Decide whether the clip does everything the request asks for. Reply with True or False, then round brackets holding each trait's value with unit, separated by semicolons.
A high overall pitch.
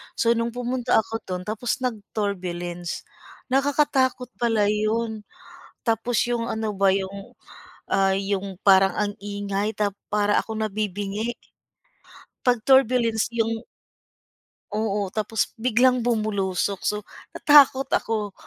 True (215 Hz)